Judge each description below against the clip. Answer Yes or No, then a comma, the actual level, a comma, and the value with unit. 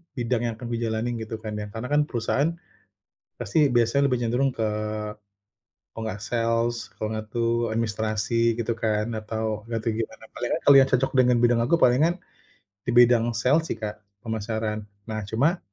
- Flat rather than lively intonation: Yes, narrow, 1.9 semitones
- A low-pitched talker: Yes, low, 115 Hz